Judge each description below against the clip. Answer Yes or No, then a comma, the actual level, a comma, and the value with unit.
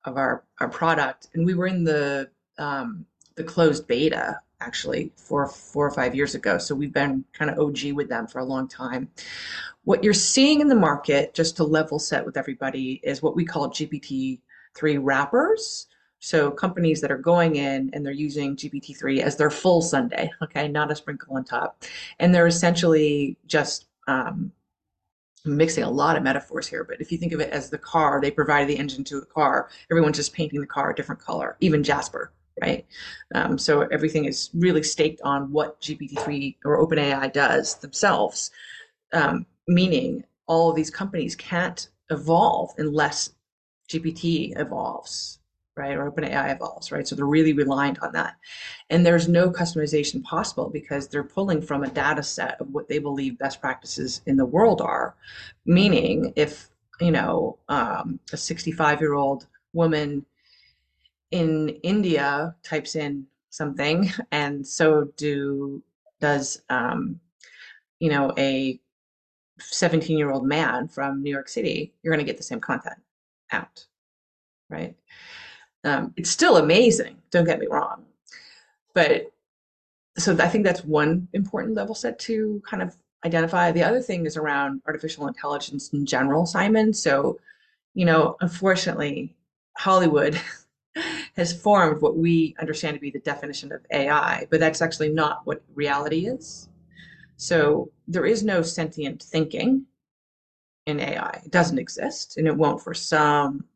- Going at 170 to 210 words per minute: No, average, 160 wpm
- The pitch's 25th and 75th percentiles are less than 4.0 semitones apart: Yes, average, 3.3 semitones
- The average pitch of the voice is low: No, medium, 155 Hz